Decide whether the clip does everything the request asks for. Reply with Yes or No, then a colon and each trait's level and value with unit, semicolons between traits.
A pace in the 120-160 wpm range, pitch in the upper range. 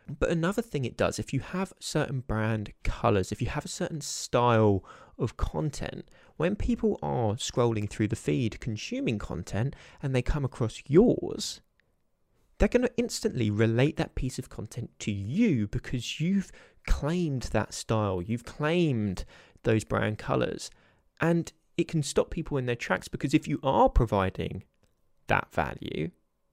No: average, 155 wpm; low, 125 Hz